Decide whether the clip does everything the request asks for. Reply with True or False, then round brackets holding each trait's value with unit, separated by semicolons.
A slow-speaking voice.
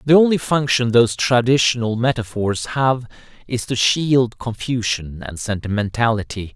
True (120 wpm)